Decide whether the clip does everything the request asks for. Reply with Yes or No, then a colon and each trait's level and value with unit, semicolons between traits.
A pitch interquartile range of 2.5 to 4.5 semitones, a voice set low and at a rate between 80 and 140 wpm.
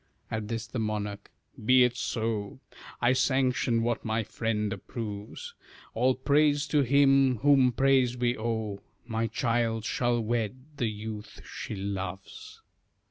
Yes: average, 3.0 semitones; low, 115 Hz; slow, 135 wpm